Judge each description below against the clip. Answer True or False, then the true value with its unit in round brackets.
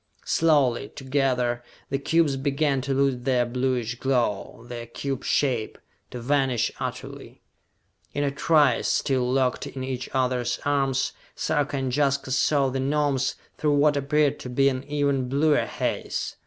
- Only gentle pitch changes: True (2.2 semitones)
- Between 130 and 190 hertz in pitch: True (135 Hz)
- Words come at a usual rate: True (145 wpm)